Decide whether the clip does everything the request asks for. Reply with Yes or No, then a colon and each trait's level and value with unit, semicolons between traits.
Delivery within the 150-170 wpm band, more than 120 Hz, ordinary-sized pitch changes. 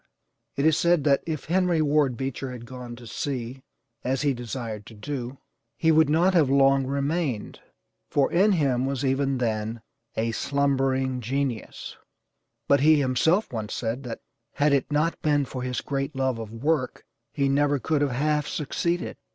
Yes: average, 165 wpm; low, 135 Hz; average, 3.0 semitones